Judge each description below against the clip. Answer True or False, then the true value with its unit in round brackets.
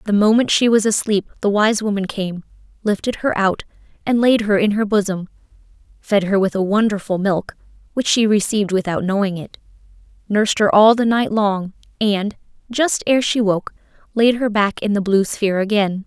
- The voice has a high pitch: True (205 Hz)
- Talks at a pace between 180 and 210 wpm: True (185 wpm)